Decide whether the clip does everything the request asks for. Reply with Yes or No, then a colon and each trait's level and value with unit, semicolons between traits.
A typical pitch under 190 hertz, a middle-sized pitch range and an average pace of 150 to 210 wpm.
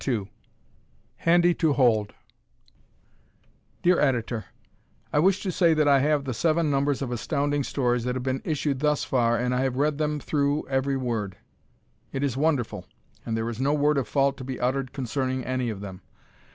Yes: low, 135 Hz; average, 3.1 semitones; average, 180 wpm